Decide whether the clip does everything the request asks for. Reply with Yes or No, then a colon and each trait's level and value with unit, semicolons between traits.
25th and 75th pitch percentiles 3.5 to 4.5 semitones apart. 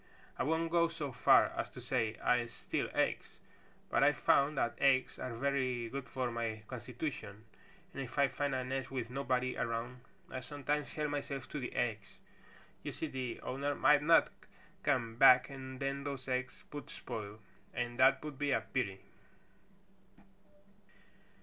No: narrow, 2.6 semitones